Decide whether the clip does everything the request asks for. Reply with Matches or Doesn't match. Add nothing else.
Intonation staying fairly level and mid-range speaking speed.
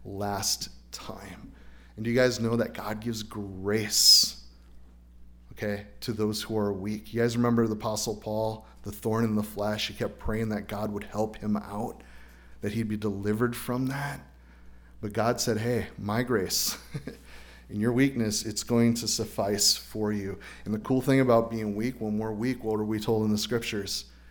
Matches